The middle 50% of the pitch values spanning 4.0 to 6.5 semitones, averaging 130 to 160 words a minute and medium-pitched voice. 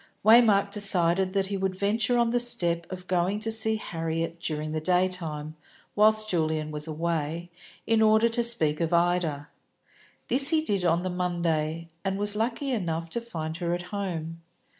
No: average, 4.6 semitones; average, 170 wpm; medium, 180 Hz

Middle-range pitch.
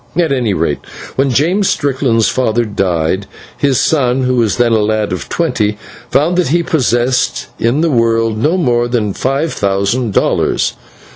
No: low, 120 Hz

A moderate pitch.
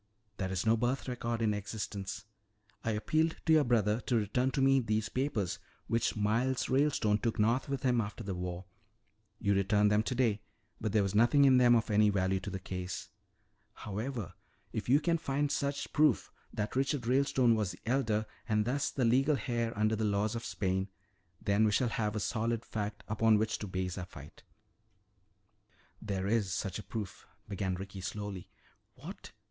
No: low, 110 Hz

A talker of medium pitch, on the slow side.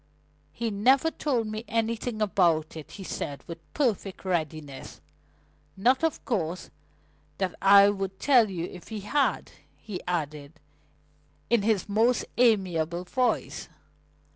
No: high, 200 Hz; slow, 125 wpm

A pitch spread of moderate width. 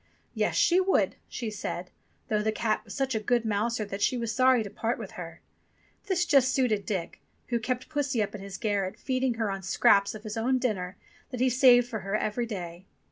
Yes: average, 3.8 semitones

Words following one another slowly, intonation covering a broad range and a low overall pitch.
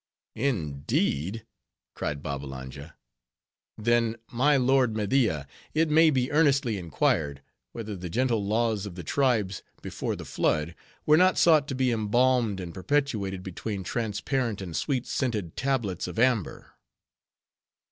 Yes: slow, 125 wpm; wide, 6.2 semitones; low, 110 Hz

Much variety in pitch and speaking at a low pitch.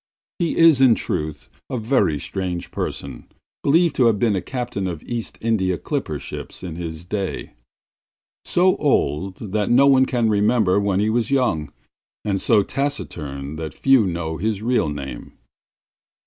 Yes: wide, 6.6 semitones; low, 105 Hz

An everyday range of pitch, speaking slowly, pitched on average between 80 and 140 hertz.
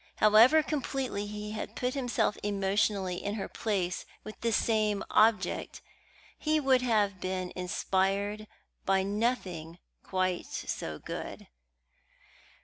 No: average, 3.2 semitones; slow, 115 wpm; high, 205 Hz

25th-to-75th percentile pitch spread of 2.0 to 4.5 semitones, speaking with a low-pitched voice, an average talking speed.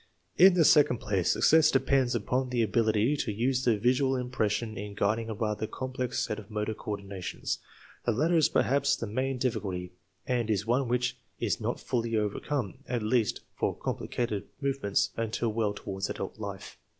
Yes: average, 3.5 semitones; low, 115 Hz; average, 170 wpm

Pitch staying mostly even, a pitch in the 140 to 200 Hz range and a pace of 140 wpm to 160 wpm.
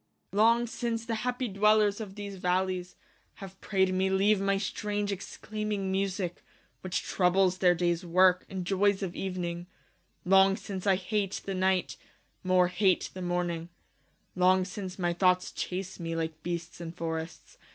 Yes: narrow, 1.9 semitones; high, 190 Hz; average, 155 wpm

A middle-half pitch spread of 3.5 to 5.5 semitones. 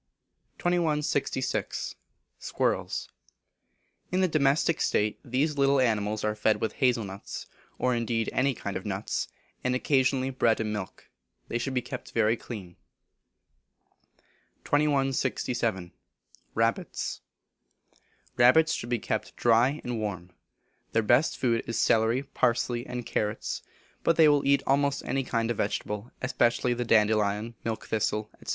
Yes: average, 3.9 semitones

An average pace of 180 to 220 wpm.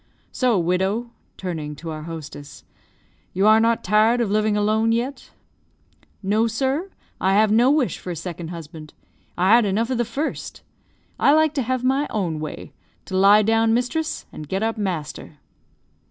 No: average, 170 wpm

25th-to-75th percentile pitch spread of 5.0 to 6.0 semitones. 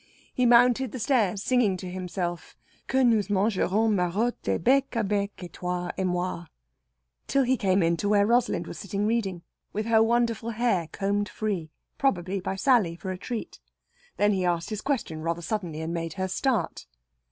No: average, 4.5 semitones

